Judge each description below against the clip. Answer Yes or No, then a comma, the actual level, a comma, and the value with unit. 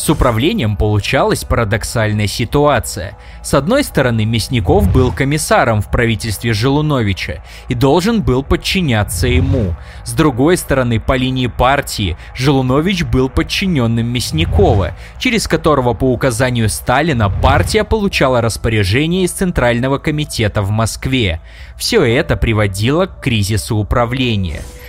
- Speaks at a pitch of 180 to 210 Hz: No, low, 120 Hz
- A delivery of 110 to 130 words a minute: Yes, average, 115 wpm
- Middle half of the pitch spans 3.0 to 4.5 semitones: No, average, 4.9 semitones